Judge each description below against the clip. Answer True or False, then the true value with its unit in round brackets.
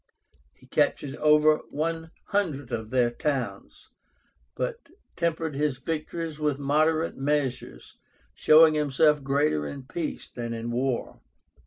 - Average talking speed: False (120 wpm)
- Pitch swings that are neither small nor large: True (3.0 semitones)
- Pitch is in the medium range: True (150 Hz)